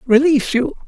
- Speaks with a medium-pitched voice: No, very high, 265 Hz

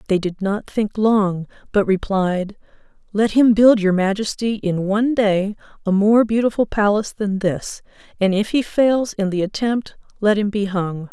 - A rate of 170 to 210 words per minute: Yes, average, 175 wpm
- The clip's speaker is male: No, female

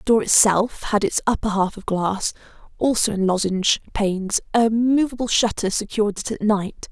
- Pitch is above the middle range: Yes, high, 210 Hz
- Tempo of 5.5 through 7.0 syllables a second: No, 5.1 syllables/s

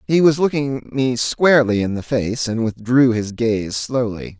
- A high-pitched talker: No, low, 120 Hz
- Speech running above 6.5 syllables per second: No, 4.3 syllables/s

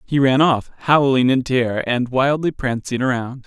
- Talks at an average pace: Yes, average, 175 wpm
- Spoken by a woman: No, male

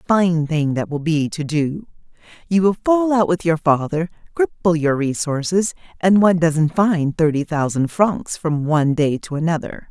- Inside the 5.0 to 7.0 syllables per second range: No, 4.8 syllables/s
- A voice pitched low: No, medium, 165 Hz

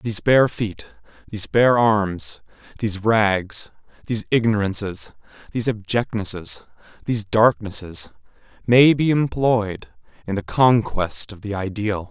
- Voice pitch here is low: Yes, low, 105 Hz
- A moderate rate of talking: No, slow, 115 wpm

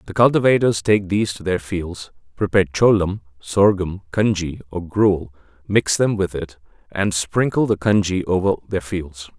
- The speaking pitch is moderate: No, very low, 95 Hz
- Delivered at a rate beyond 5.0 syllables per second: No, 4.8 syllables/s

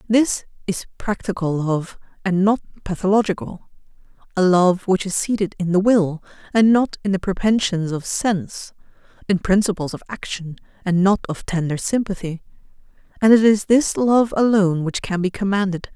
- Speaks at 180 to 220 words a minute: No, average, 155 wpm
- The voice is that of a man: No, female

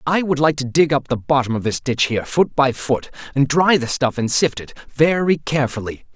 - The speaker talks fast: Yes, fast, 215 wpm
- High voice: No, medium, 140 Hz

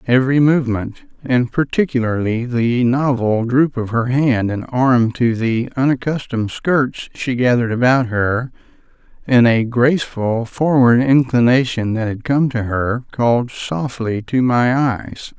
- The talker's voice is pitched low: Yes, low, 125 Hz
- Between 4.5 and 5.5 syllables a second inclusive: No, 4.2 syllables/s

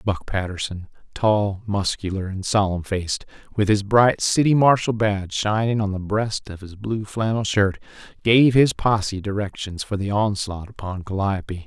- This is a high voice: No, low, 105 Hz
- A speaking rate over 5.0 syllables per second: No, 4.7 syllables/s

